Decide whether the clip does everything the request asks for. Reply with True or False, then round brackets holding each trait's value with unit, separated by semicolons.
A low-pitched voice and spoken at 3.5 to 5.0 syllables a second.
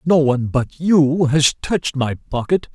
False (145 Hz; 4.3 syllables/s)